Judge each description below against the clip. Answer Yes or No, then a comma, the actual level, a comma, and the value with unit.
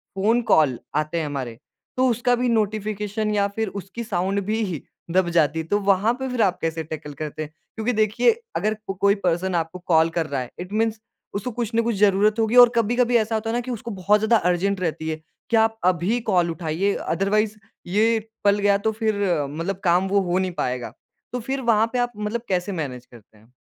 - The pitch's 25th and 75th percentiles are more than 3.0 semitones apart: Yes, average, 4.6 semitones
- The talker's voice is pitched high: Yes, high, 200 Hz